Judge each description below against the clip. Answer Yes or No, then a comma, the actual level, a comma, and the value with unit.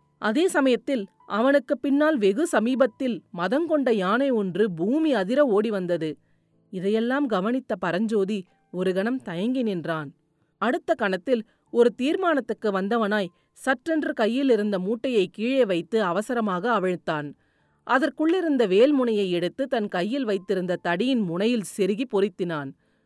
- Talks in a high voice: Yes, high, 220 Hz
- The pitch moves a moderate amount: No, wide, 5.8 semitones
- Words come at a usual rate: Yes, average, 110 wpm